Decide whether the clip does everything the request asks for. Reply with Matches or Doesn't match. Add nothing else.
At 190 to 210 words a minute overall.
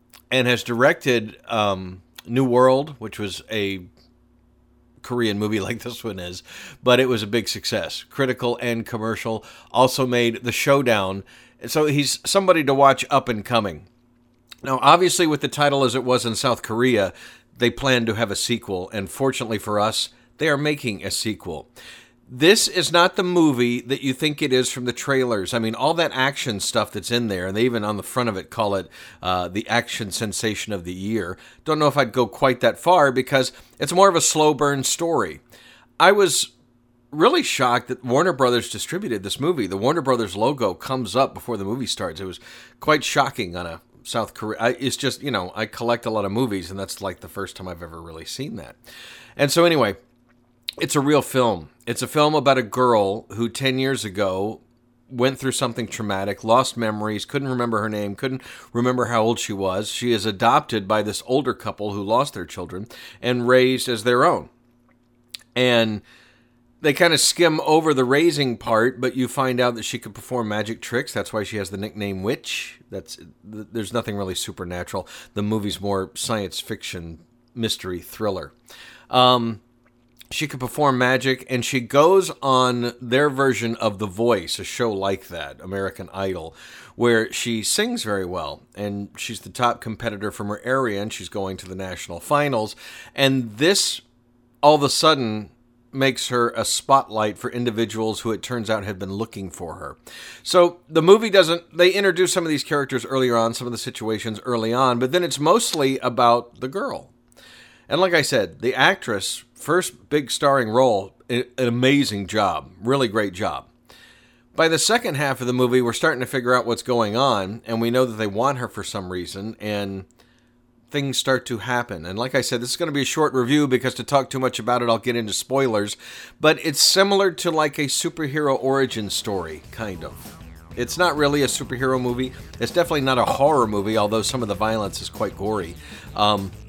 Matches